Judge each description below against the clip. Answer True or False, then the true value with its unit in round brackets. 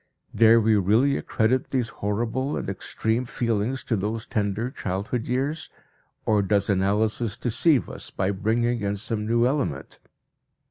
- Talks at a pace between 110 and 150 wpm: True (140 wpm)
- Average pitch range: True (3.2 semitones)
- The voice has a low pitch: True (110 Hz)